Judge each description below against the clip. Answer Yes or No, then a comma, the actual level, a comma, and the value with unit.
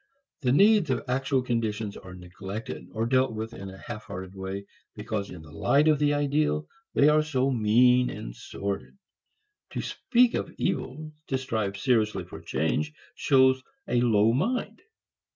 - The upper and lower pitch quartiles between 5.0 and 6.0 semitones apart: Yes, wide, 5.4 semitones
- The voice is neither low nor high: No, low, 120 Hz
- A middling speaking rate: Yes, average, 160 wpm